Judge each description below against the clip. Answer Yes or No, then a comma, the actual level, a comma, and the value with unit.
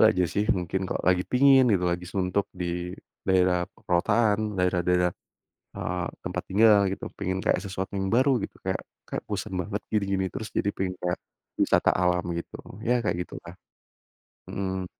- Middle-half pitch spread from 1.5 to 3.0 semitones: Yes, narrow, 2.5 semitones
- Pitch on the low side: Yes, very low, 95 Hz